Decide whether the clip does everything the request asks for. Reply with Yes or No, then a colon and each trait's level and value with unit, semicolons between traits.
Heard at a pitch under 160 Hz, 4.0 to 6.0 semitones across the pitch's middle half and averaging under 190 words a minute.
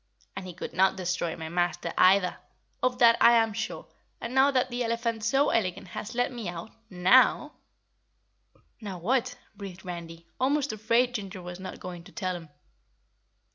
No: high, 200 Hz; average, 5.2 semitones; average, 175 wpm